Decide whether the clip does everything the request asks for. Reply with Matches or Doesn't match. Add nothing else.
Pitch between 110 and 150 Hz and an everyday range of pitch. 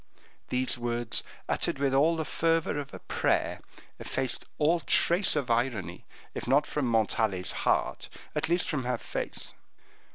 Matches